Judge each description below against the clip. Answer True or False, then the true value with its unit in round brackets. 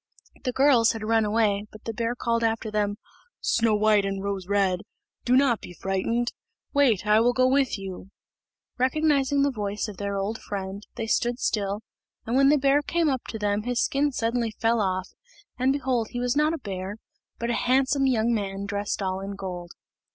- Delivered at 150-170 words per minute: False (195 wpm)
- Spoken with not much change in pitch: False (4.1 semitones)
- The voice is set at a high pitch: True (225 Hz)